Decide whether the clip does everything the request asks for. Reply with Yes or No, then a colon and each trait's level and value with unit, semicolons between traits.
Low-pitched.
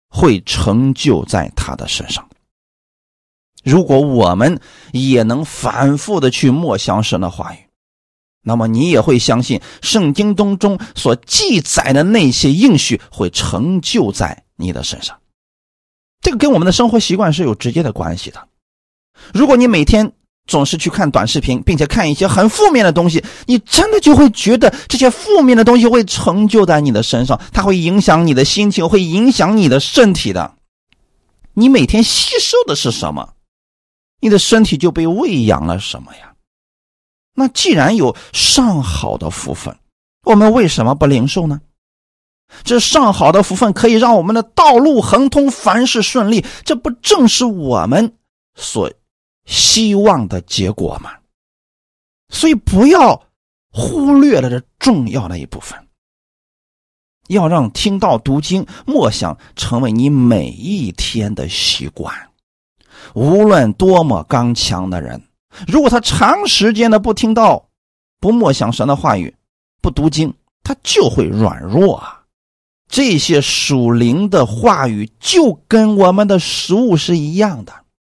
No: medium, 175 Hz